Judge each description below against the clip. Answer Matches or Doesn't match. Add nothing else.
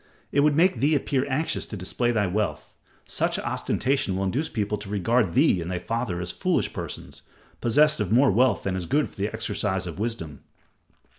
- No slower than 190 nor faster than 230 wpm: Matches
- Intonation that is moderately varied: Doesn't match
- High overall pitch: Doesn't match